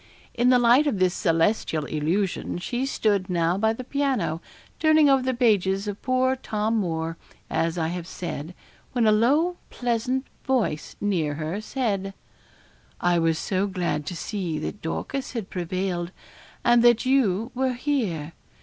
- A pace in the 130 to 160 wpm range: Yes, average, 155 wpm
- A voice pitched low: No, high, 205 Hz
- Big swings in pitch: Yes, wide, 6.3 semitones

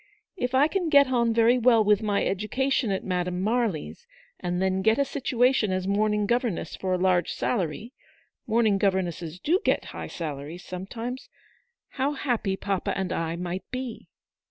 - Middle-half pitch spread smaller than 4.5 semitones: No, average, 5.1 semitones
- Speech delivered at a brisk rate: No, average, 170 wpm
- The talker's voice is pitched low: No, high, 210 Hz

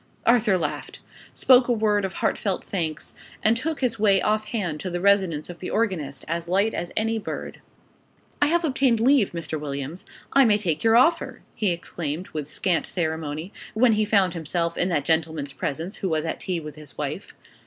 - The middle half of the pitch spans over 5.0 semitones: Yes, wide, 5.4 semitones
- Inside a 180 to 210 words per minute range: Yes, average, 190 wpm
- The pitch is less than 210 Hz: Yes, medium, 185 Hz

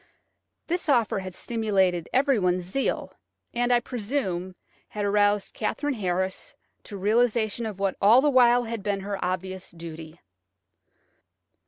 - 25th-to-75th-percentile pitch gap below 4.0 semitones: No, average, 4.5 semitones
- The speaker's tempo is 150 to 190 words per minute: No, slow, 135 wpm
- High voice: Yes, high, 205 Hz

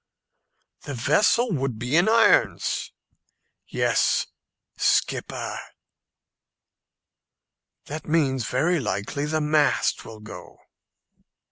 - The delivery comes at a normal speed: No, slow, 85 wpm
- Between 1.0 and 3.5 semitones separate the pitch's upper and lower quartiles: No, average, 4.5 semitones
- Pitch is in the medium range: Yes, medium, 145 Hz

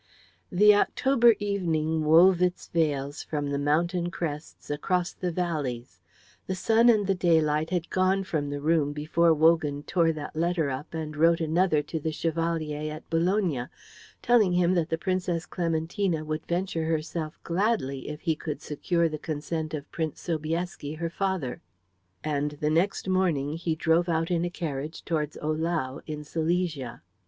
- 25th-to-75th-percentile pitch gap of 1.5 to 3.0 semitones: Yes, narrow, 2.6 semitones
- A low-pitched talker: No, medium, 165 Hz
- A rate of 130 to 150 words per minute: No, average, 160 wpm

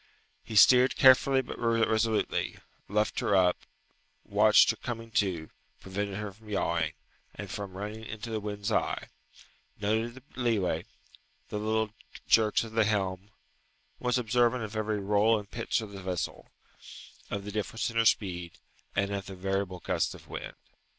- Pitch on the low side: Yes, low, 105 Hz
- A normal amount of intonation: No, narrow, 2.3 semitones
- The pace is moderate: Yes, average, 155 wpm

